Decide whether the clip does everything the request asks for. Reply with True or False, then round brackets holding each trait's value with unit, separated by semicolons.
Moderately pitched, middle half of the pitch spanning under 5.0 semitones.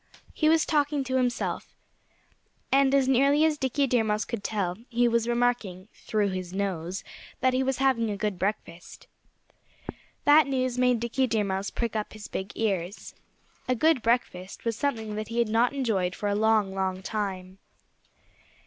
False (225 Hz; 4.5 semitones)